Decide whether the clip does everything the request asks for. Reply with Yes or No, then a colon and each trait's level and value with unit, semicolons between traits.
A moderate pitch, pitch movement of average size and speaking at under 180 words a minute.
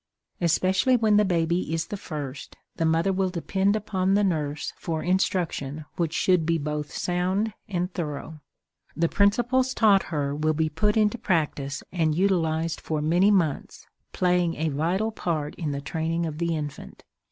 Yes: medium, 170 Hz; average, 3.6 semitones; average, 165 wpm